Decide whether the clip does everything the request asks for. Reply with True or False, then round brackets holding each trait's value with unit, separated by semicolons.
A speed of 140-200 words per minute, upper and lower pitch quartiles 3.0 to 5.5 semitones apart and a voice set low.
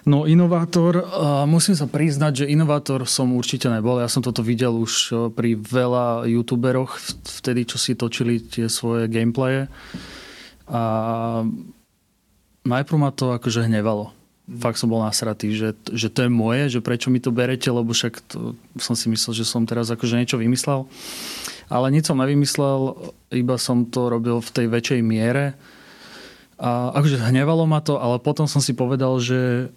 False (160 wpm; 2.5 semitones; 125 Hz)